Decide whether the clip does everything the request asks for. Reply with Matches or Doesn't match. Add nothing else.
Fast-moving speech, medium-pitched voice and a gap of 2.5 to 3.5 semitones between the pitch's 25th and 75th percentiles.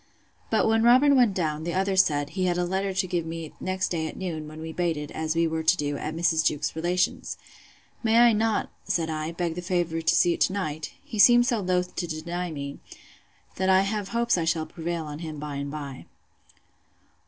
Matches